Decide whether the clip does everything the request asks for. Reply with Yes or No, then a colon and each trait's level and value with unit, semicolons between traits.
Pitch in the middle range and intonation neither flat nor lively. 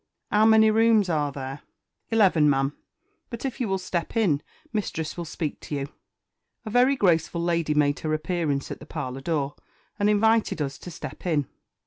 No: medium, 170 Hz; wide, 6.4 semitones